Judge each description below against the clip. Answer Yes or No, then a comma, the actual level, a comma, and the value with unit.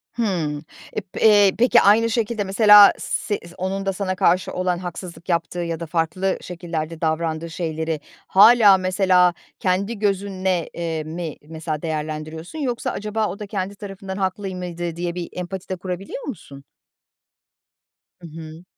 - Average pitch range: Yes, average, 3.2 semitones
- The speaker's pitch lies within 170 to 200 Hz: Yes, medium, 185 Hz